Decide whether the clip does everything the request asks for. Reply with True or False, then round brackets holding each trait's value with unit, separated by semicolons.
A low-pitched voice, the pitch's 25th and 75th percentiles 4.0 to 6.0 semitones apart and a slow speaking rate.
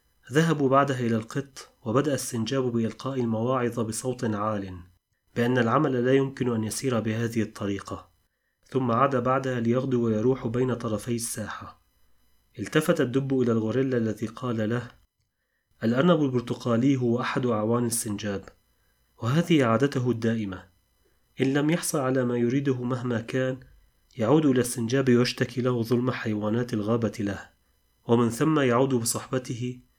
False (120 Hz; 2.6 semitones; 125 wpm)